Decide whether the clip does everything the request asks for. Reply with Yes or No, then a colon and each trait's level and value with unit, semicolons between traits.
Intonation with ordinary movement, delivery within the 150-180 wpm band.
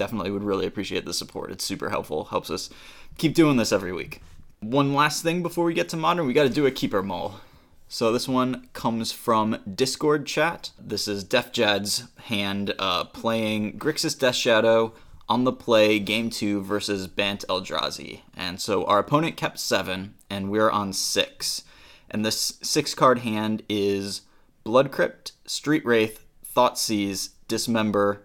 Yes: average, 4.1 semitones; average, 165 wpm